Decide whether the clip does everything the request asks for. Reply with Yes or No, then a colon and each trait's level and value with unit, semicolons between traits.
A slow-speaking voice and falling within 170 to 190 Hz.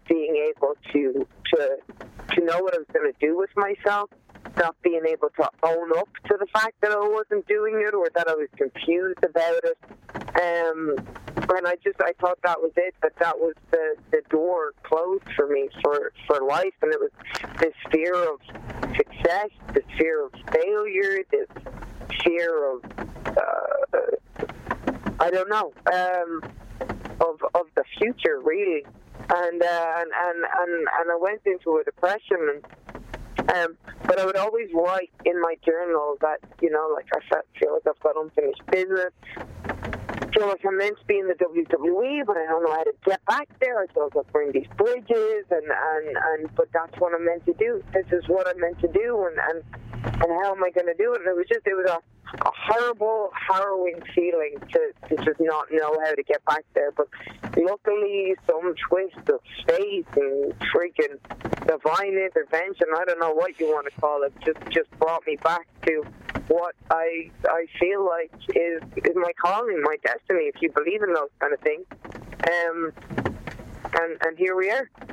No: average, 185 wpm; medium, 185 Hz